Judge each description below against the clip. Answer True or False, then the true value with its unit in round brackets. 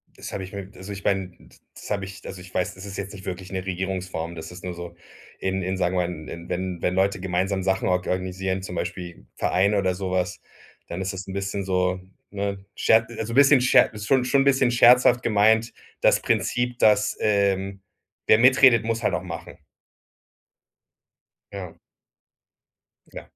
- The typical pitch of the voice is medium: False (95 Hz)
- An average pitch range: False (2.3 semitones)